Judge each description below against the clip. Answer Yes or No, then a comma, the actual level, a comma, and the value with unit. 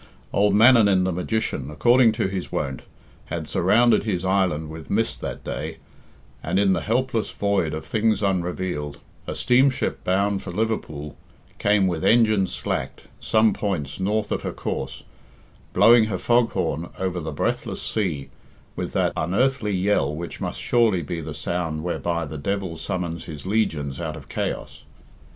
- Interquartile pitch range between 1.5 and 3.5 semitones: No, average, 4.9 semitones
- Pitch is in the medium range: No, very low, 95 Hz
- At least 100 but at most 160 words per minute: Yes, average, 155 wpm